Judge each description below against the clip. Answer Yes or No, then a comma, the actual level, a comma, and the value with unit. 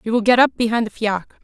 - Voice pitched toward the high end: Yes, high, 225 Hz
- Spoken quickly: Yes, fast, 295 wpm